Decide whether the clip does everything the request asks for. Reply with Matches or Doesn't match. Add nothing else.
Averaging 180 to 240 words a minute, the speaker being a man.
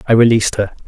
Matches